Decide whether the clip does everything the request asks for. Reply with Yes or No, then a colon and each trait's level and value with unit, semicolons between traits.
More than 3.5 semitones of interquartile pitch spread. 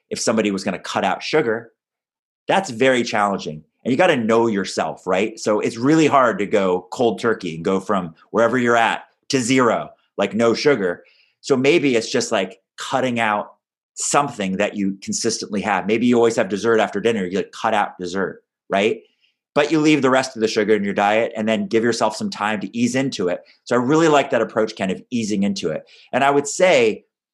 Yes: average, 4.5 semitones